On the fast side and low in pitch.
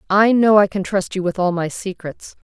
No: fast, 240 wpm; high, 195 Hz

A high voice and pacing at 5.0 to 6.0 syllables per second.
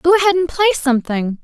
No: very high, 295 Hz; 7.0 syllables/s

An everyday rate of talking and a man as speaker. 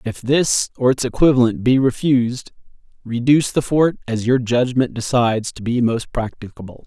Yes: average, 155 wpm; male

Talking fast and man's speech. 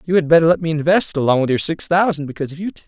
Yes: fast, 415 wpm; male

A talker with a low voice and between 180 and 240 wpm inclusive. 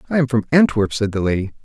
No: low, 115 Hz; fast, 255 wpm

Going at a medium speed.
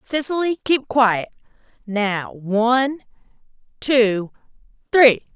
No: slow, 55 wpm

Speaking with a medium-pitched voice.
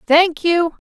No: very high, 335 Hz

